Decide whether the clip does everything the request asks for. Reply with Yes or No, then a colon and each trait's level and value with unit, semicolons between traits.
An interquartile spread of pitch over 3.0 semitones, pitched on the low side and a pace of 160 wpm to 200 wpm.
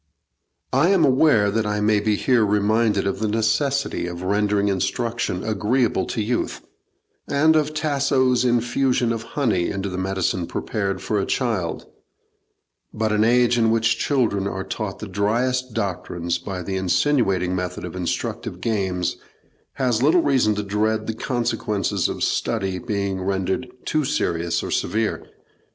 No: average, 4.1 semitones; low, 110 Hz; average, 145 wpm